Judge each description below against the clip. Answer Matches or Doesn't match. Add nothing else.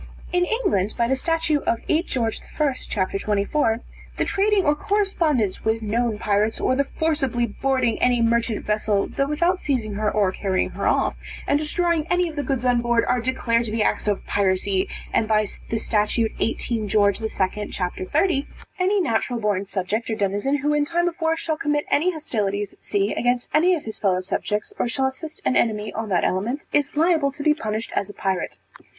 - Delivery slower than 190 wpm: Doesn't match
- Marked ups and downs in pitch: Matches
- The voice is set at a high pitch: Matches